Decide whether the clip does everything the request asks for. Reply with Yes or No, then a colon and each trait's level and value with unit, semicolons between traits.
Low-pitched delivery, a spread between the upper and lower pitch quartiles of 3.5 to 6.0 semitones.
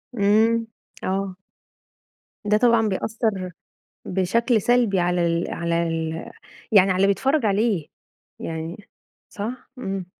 No: high, 195 Hz; average, 4.0 semitones